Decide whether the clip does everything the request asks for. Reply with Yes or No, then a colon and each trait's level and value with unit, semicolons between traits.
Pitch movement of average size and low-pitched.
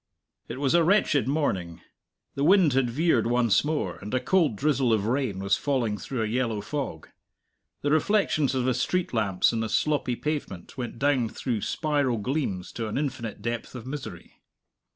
Yes: average, 4.7 semitones; low, 130 Hz